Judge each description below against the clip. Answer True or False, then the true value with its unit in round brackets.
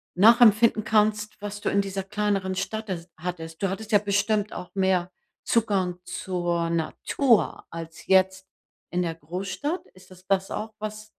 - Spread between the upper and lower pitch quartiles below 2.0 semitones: False (2.8 semitones)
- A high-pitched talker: True (195 Hz)